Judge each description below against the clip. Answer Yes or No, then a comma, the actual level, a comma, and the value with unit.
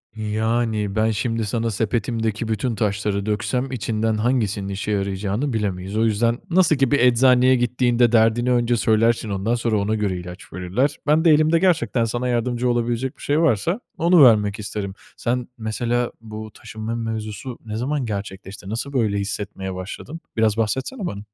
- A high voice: No, low, 115 Hz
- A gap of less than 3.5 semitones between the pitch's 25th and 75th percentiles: Yes, average, 2.9 semitones